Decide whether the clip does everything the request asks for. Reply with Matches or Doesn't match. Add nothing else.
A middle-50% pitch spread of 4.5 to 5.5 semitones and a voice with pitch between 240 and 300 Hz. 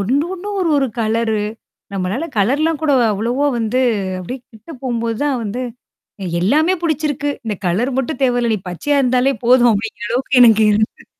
Matches